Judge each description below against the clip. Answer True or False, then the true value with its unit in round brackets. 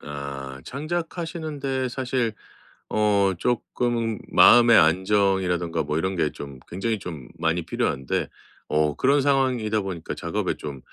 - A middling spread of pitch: False (7.7 semitones)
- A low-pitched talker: True (100 Hz)